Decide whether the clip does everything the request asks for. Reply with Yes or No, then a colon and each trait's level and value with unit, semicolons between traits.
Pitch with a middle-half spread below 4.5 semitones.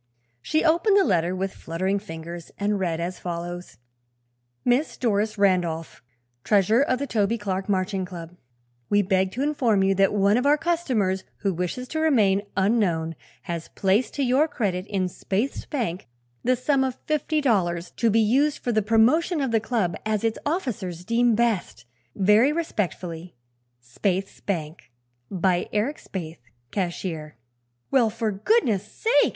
No: wide, 5.4 semitones